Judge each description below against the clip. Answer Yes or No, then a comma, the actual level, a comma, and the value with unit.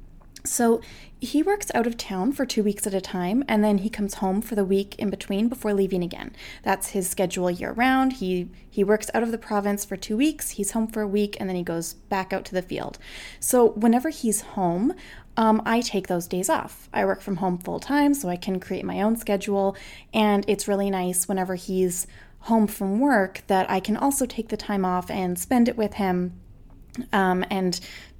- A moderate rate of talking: No, fast, 215 wpm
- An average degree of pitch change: Yes, average, 3.3 semitones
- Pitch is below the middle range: No, high, 205 Hz